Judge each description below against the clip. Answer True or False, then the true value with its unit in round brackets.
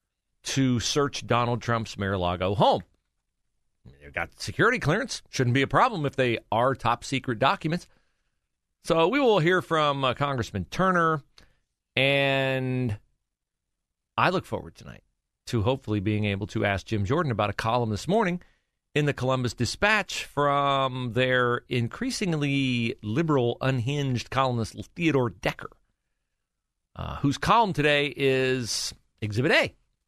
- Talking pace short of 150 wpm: True (140 wpm)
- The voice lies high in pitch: False (125 Hz)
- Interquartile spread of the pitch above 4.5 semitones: True (5.0 semitones)